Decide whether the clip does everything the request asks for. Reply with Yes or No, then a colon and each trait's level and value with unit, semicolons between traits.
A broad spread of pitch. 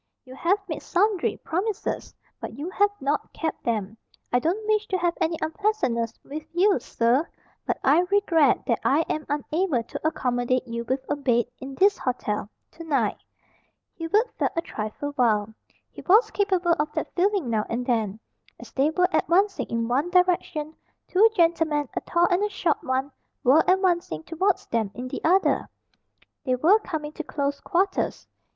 Yes: wide, 6.4 semitones